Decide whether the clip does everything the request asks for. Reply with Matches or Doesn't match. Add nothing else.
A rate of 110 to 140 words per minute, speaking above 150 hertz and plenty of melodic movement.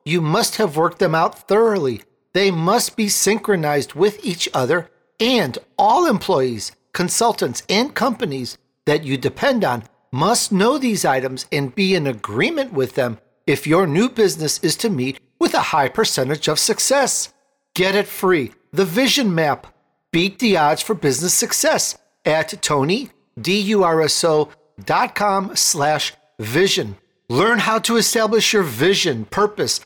Matches